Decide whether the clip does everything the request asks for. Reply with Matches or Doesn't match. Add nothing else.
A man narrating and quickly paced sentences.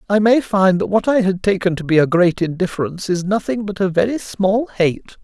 Matches